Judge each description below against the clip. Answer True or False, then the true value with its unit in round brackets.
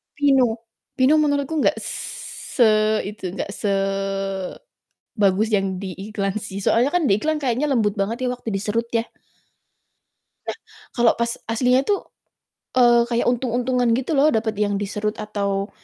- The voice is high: True (230 Hz)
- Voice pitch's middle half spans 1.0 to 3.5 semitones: False (4.4 semitones)